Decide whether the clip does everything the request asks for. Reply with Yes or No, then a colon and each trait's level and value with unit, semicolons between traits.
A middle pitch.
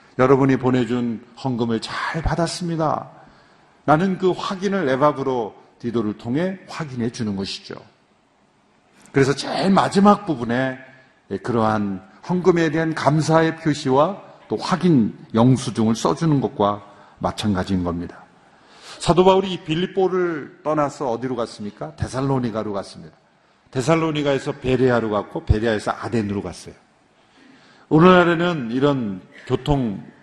No: low, 130 Hz